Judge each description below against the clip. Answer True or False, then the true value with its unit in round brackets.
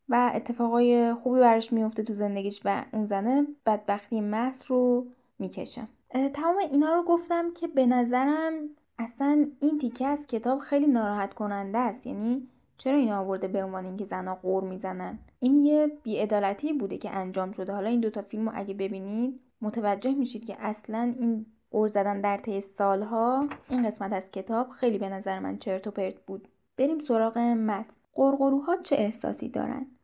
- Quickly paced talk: True (165 wpm)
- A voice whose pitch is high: True (230 Hz)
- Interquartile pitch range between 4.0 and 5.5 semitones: True (4.7 semitones)